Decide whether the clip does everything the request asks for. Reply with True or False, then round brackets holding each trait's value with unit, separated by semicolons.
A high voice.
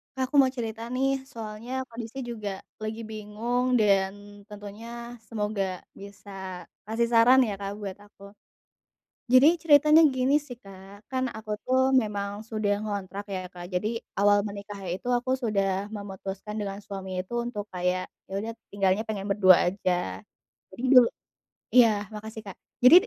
True (210 Hz)